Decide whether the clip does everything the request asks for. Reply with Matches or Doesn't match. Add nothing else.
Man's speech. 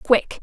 Doesn't match